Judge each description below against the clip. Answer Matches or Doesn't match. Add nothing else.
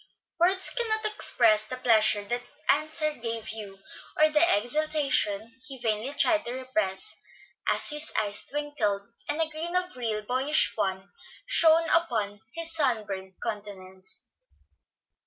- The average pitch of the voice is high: Matches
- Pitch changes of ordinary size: Doesn't match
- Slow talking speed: Matches